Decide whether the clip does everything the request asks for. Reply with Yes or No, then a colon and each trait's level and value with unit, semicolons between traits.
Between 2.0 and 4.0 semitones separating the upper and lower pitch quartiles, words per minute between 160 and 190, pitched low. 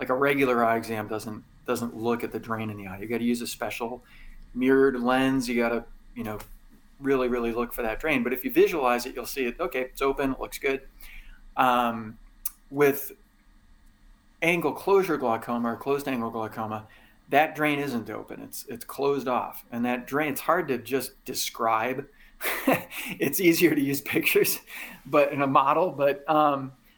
Yes: average, 3.6 semitones; average, 185 wpm; low, 125 Hz